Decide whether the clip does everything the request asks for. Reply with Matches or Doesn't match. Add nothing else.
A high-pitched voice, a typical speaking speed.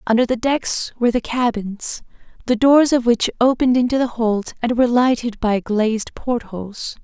Matches